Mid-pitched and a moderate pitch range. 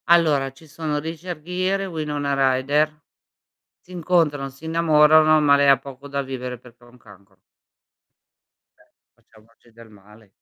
Yes: medium, 145 Hz; average, 3.9 semitones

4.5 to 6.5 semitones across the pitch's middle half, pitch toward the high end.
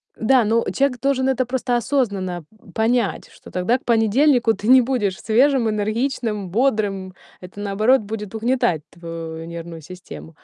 Yes: average, 5.0 semitones; high, 220 Hz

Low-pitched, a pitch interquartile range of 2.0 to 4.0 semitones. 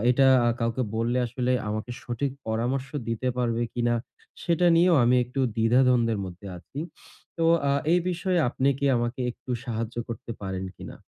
Yes: low, 120 Hz; average, 2.7 semitones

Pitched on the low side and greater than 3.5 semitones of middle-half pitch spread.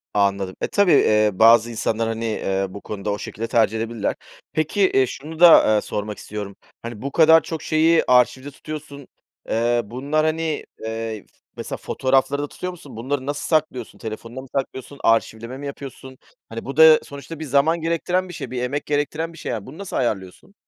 Yes: low, 130 Hz; wide, 5.6 semitones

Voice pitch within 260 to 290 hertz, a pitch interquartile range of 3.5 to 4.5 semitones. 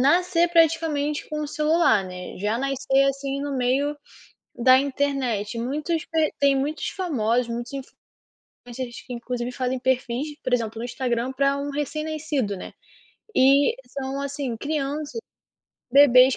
No: very high, 275 Hz; average, 3.1 semitones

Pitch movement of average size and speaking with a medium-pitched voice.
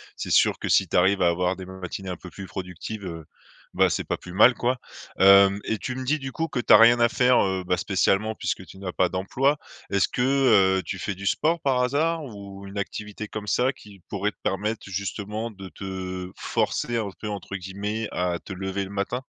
No: average, 3.9 semitones; low, 100 Hz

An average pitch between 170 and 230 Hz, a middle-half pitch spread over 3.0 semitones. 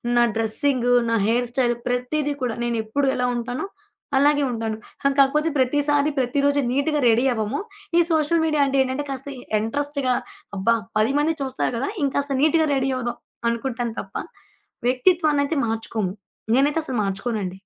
No: very high, 260 Hz; average, 3.5 semitones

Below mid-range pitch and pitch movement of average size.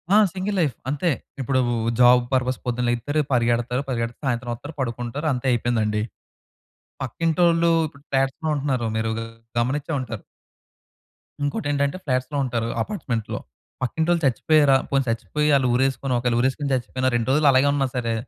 Yes: low, 130 Hz; average, 3.3 semitones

